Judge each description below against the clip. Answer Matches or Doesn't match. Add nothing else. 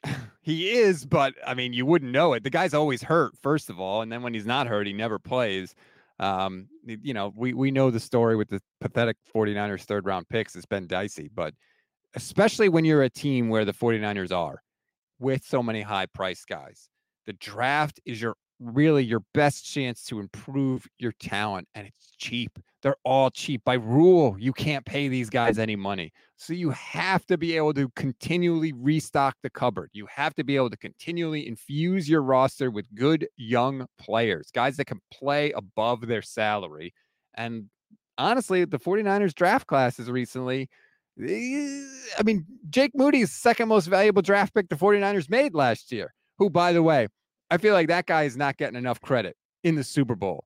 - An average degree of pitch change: Doesn't match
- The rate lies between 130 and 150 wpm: Doesn't match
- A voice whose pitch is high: Doesn't match